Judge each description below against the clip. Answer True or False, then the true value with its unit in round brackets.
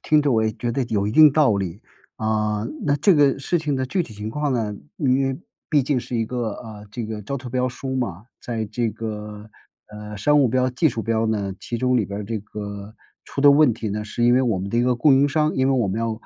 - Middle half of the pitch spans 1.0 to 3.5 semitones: False (3.9 semitones)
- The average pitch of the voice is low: True (115 Hz)